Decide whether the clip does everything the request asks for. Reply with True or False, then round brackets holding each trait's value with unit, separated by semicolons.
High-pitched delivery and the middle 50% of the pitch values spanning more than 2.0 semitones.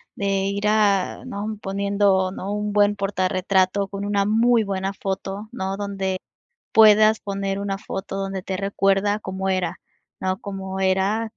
False (195 Hz; 1.2 semitones)